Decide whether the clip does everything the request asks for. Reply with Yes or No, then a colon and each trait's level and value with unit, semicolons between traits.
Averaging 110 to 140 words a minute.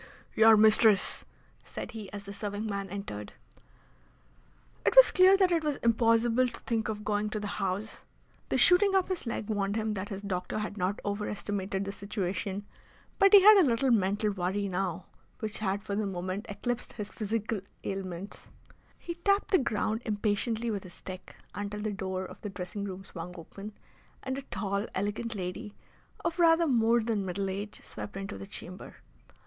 No: average, 175 wpm